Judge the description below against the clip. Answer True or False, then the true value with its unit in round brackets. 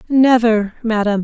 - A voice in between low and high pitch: False (225 Hz)